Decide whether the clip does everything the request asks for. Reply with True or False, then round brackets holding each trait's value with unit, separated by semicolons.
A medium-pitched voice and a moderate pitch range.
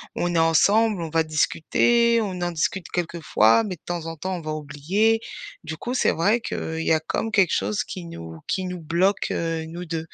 True (170 Hz; 3.7 semitones)